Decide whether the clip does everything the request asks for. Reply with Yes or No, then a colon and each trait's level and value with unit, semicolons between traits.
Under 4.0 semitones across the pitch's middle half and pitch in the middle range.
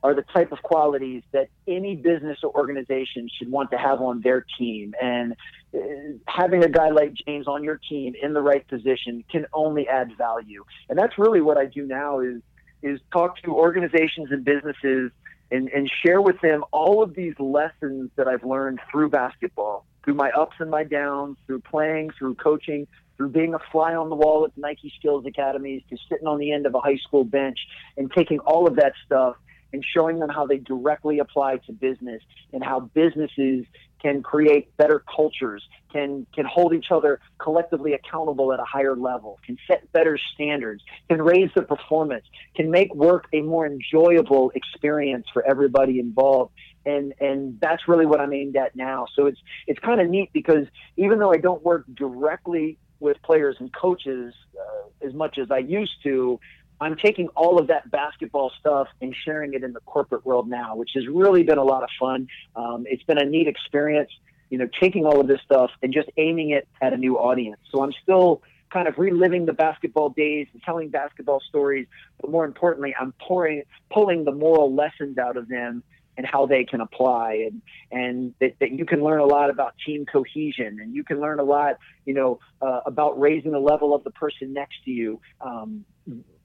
Yes: average, 3.1 semitones; medium, 145 Hz